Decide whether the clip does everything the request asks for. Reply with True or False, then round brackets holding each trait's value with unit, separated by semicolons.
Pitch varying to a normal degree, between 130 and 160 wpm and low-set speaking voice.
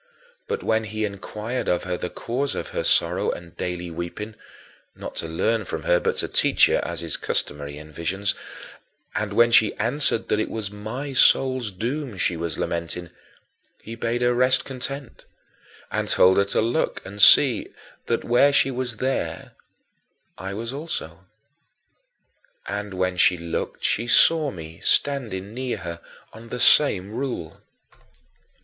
False (5.7 semitones; 155 wpm; 110 Hz)